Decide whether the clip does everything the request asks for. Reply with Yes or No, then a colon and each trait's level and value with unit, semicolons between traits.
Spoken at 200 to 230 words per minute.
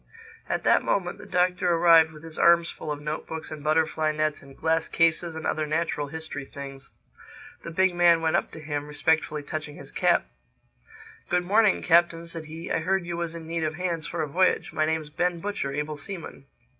Yes: fast, 205 wpm